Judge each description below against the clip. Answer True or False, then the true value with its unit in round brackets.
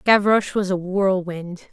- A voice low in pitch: False (190 Hz)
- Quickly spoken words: False (140 wpm)